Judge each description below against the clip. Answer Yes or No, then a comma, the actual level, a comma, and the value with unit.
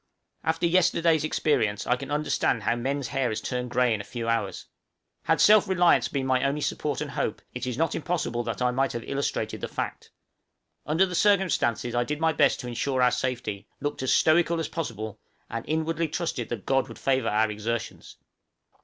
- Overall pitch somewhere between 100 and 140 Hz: Yes, low, 135 Hz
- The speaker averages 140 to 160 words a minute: No, average, 195 wpm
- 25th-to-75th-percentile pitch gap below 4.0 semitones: No, average, 5.0 semitones